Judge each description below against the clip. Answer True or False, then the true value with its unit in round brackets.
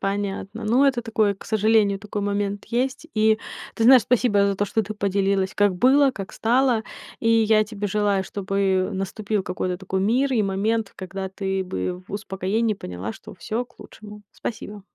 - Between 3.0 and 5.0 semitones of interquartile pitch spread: False (2.5 semitones)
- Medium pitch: False (205 Hz)